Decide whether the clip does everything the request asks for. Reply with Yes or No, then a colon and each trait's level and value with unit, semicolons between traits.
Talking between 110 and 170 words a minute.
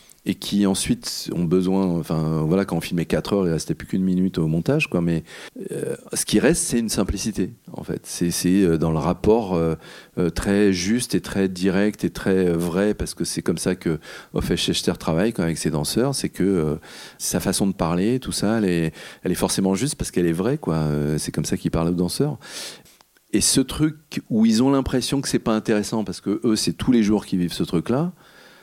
No: fast, 220 wpm